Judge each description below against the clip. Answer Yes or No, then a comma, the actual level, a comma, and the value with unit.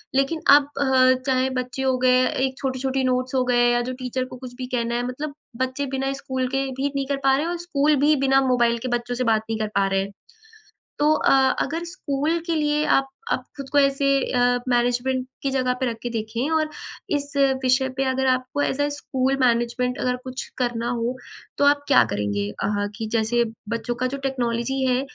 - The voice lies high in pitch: Yes, very high, 255 Hz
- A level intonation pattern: Yes, narrow, 2.0 semitones